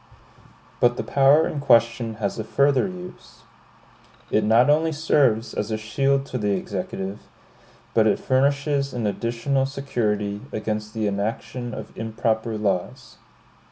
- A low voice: Yes, low, 115 Hz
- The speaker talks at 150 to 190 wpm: No, slow, 135 wpm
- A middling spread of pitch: Yes, average, 4.4 semitones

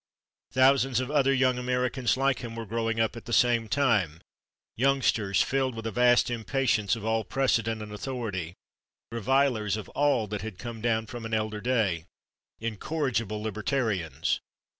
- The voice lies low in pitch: Yes, low, 115 Hz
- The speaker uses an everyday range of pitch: Yes, average, 3.1 semitones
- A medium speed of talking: Yes, average, 160 wpm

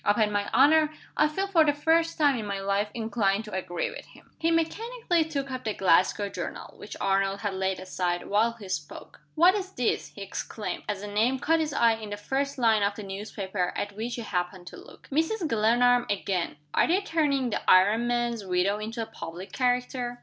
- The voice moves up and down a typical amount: No, wide, 6.0 semitones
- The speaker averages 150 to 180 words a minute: No, fast, 205 wpm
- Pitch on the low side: No, high, 225 Hz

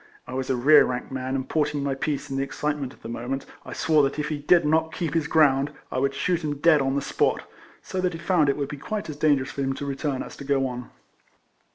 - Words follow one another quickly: Yes, fast, 270 wpm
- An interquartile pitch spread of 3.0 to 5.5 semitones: No, narrow, 2.4 semitones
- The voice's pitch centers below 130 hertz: No, medium, 140 Hz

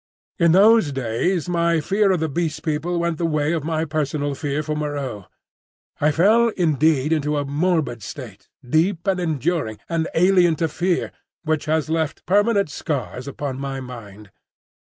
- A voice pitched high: No, medium, 155 Hz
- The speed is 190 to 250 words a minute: No, average, 160 wpm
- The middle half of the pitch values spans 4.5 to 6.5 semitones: No, average, 3.4 semitones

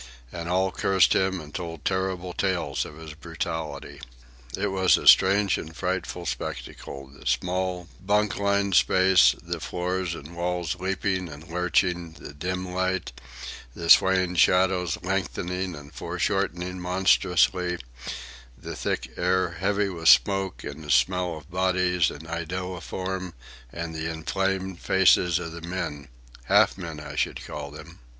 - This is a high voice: No, very low, 90 Hz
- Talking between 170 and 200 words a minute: No, average, 140 wpm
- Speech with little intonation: Yes, narrow, 2.3 semitones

